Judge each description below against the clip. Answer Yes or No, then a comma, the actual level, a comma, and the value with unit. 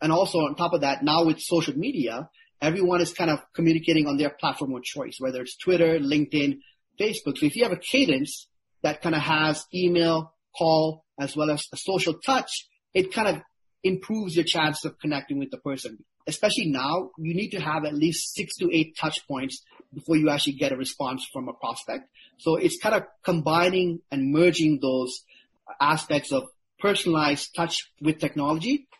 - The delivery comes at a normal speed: Yes, average, 185 wpm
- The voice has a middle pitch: Yes, medium, 160 Hz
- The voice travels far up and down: No, average, 3.2 semitones